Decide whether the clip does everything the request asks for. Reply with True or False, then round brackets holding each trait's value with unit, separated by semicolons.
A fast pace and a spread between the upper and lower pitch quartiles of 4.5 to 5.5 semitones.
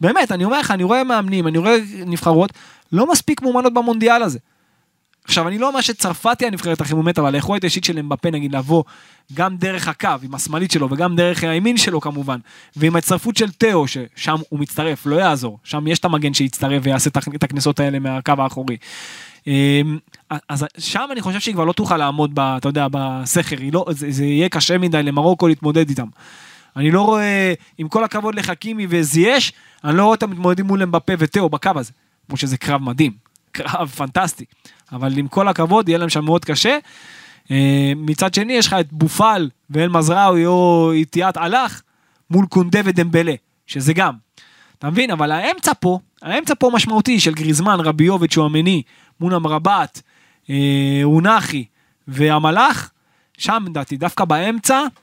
True (170 wpm; 4.8 semitones)